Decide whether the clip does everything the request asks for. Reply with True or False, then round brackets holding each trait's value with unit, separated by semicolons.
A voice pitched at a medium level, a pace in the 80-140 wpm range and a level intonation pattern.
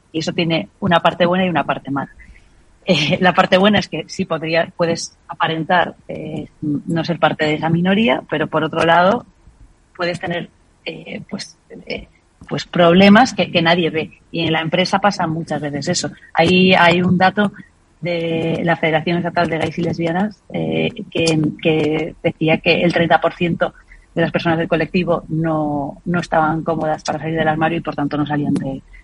False (165 Hz; 180 wpm; 1.9 semitones)